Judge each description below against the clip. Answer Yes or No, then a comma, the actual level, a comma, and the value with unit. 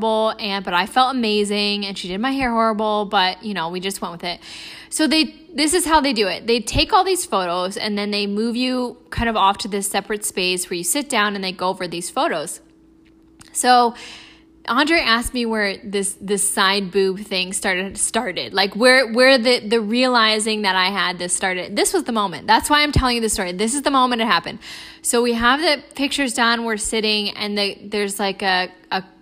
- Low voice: No, high, 215 Hz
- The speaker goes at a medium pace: No, fast, 220 wpm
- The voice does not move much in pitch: No, average, 4.5 semitones